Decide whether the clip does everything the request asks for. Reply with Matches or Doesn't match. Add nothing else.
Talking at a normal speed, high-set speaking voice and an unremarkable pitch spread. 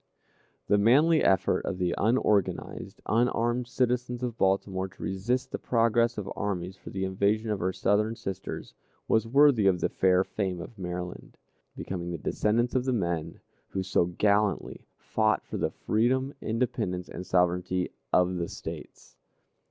Doesn't match